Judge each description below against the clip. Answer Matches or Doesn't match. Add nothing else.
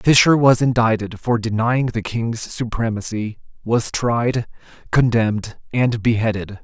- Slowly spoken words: Matches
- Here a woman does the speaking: Doesn't match